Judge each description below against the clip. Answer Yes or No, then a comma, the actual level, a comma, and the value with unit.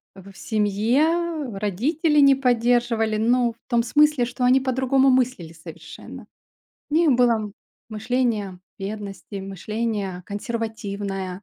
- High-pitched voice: Yes, high, 230 Hz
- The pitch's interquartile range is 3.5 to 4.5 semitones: Yes, average, 4.2 semitones